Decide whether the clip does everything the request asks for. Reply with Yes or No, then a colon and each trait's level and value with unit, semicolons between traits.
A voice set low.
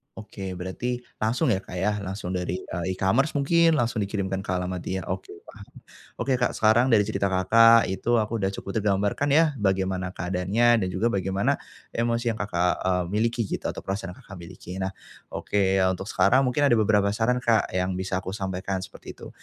Yes: low, 100 Hz